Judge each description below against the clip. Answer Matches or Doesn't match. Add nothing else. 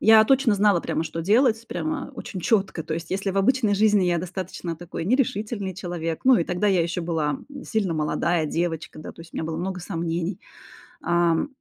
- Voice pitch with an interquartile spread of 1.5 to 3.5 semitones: Doesn't match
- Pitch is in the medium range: Matches